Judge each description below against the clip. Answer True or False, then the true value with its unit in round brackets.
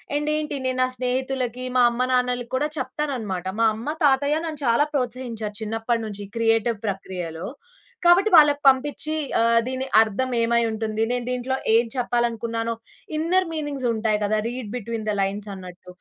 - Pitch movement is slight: False (3.3 semitones)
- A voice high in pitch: True (240 Hz)